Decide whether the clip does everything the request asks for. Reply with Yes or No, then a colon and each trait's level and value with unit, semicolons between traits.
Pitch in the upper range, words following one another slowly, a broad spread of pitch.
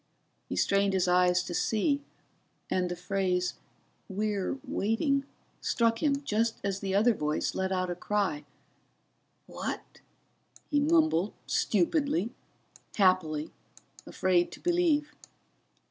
Yes: high, 200 Hz; slow, 115 wpm; wide, 6.8 semitones